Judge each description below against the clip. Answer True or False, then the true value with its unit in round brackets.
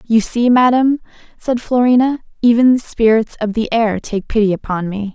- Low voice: False (230 Hz)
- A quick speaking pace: False (175 wpm)